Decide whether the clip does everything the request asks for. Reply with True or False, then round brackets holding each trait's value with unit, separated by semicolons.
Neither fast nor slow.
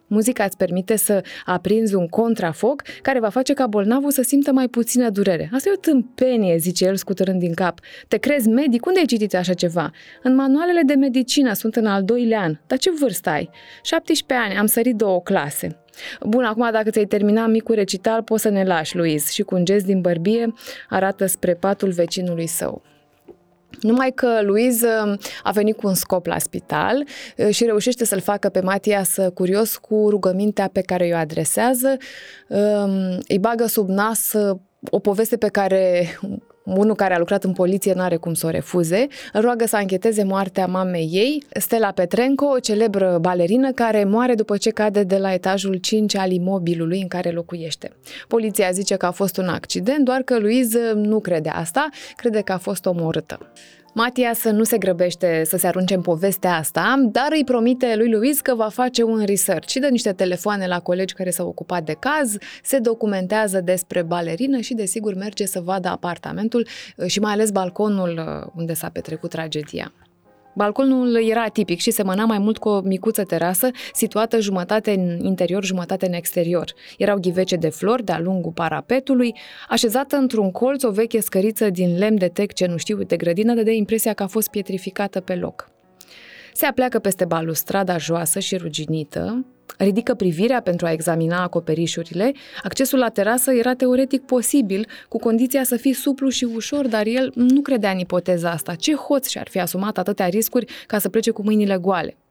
False (180 wpm)